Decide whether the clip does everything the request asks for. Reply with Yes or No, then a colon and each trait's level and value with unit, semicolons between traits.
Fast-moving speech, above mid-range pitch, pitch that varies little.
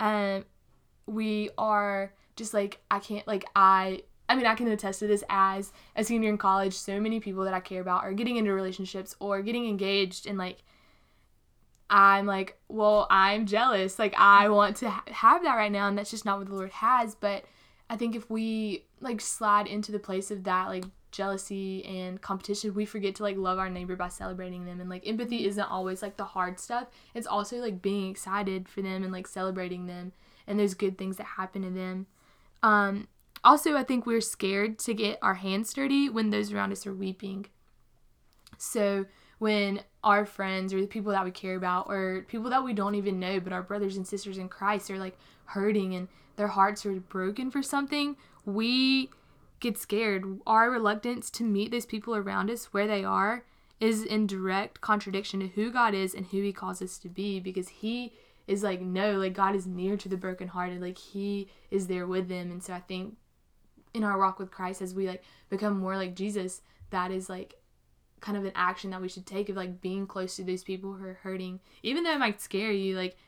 Yes: fast, 210 wpm; high, 195 Hz; narrow, 1.9 semitones